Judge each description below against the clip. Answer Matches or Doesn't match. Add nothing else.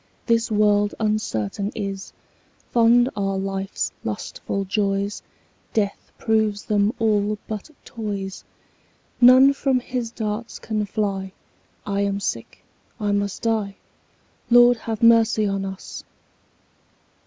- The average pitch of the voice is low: Doesn't match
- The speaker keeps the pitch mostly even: Matches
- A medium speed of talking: Doesn't match